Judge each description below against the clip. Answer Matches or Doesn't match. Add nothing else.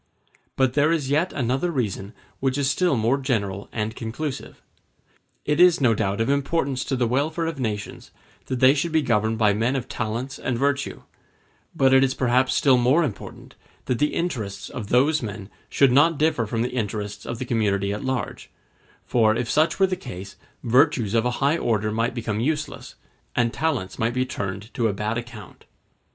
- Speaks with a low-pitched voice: Matches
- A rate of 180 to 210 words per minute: Matches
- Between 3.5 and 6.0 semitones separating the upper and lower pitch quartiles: Matches